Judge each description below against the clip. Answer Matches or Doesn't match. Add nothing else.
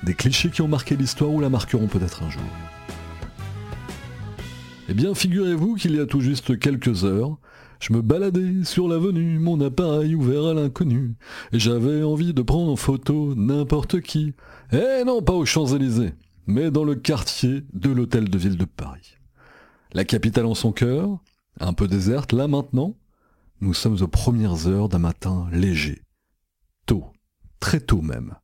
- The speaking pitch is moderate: Doesn't match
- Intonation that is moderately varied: Doesn't match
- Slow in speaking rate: Doesn't match